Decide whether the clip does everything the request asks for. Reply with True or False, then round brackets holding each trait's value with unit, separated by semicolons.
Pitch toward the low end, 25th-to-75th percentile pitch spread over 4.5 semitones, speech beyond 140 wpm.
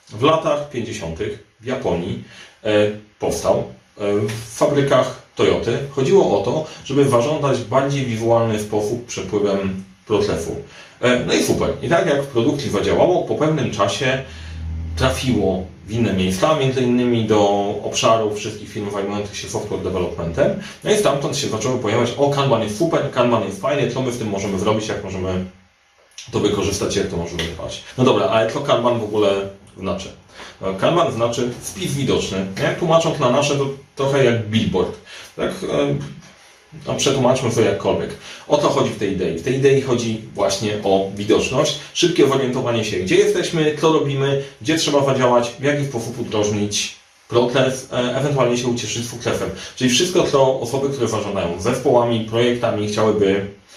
True (115 Hz; 5.1 semitones; 155 wpm)